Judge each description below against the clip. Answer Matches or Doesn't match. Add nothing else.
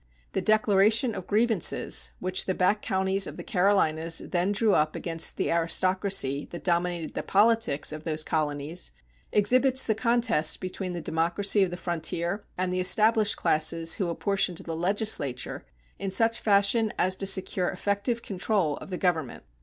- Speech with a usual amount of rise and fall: Matches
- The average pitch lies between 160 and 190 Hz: Matches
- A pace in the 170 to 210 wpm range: Doesn't match